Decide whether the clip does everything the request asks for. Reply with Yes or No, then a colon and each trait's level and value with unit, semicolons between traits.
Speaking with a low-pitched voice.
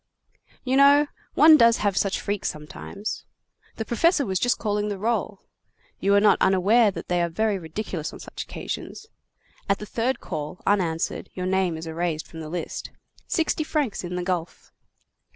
No: high, 200 Hz